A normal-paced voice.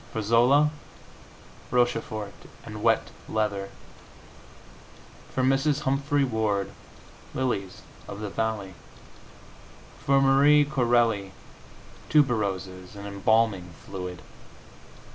No: slow, 85 wpm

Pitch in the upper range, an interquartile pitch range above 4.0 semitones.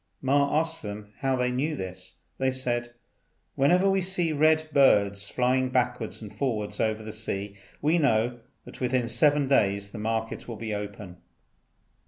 No: low, 125 Hz; average, 5.1 semitones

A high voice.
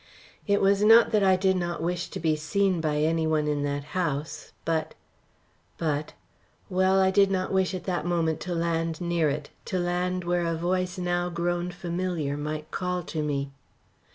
No: medium, 175 Hz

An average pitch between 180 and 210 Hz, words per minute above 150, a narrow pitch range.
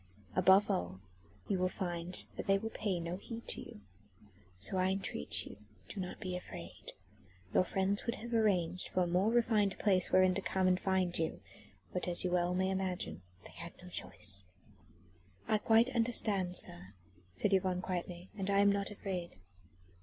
Yes: medium, 185 Hz; average, 175 wpm; narrow, 2.0 semitones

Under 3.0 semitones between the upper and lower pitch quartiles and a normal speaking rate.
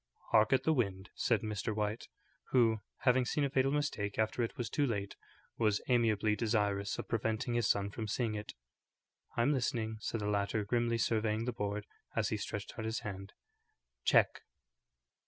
Yes: narrow, 2.4 semitones; average, 175 wpm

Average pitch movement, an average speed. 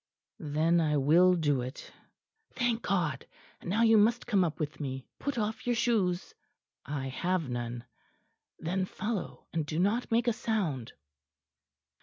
No: wide, 7.0 semitones; average, 150 wpm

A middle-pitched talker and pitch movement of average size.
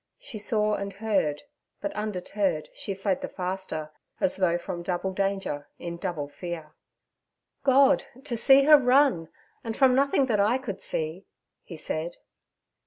No: high, 195 Hz; average, 4.7 semitones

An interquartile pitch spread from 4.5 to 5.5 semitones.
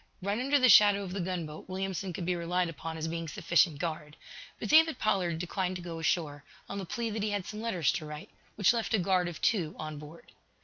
No: average, 3.7 semitones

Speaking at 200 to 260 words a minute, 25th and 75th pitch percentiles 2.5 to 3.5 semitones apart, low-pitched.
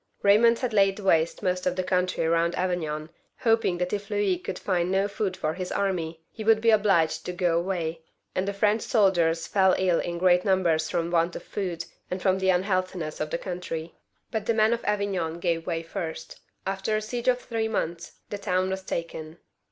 No: fast, 205 wpm; average, 3.1 semitones; medium, 185 Hz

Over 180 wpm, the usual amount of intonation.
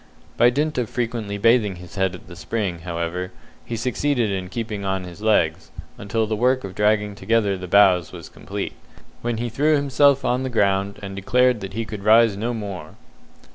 Yes: average, 190 wpm; average, 3.8 semitones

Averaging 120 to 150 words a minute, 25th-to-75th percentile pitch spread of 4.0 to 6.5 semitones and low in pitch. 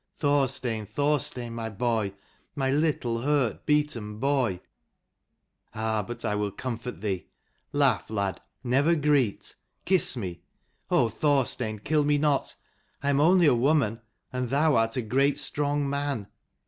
Yes: slow, 135 wpm; average, 4.4 semitones; low, 130 Hz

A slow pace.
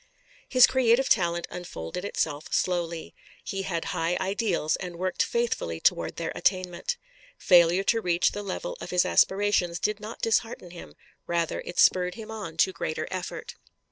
No: average, 155 wpm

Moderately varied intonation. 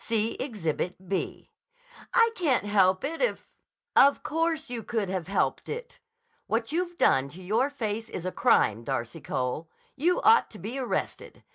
No: wide, 8.0 semitones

